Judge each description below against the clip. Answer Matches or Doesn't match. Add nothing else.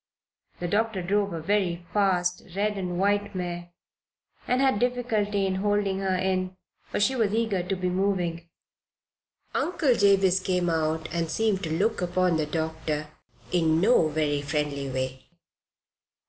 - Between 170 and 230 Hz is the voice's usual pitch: Matches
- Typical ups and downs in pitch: Matches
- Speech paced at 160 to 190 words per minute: Doesn't match